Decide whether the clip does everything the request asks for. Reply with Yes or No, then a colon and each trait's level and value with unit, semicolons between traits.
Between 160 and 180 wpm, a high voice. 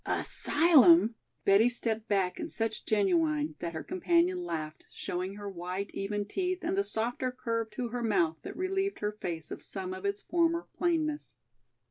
Yes: average, 165 wpm; high, 220 Hz